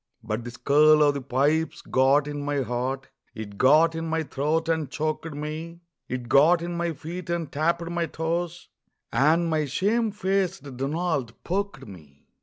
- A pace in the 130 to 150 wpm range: No, average, 165 wpm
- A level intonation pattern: No, average, 3.8 semitones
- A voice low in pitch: No, medium, 155 Hz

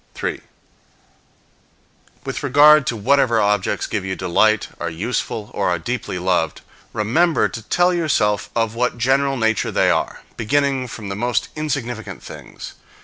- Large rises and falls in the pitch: No, average, 4.9 semitones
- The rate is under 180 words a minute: Yes, average, 145 wpm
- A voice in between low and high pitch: No, low, 115 Hz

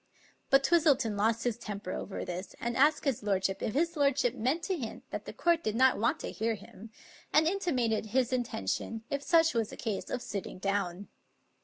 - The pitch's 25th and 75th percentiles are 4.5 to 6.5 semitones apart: Yes, average, 5.3 semitones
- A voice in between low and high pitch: No, high, 235 Hz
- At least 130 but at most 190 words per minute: No, average, 200 wpm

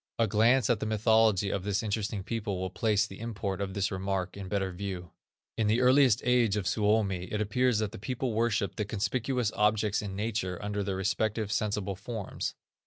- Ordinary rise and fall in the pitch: No, narrow, 2.3 semitones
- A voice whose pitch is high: No, low, 105 Hz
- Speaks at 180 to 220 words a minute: Yes, average, 190 wpm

